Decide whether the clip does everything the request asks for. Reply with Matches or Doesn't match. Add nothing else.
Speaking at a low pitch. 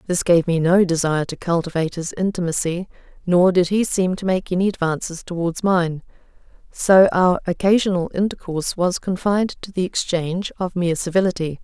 Doesn't match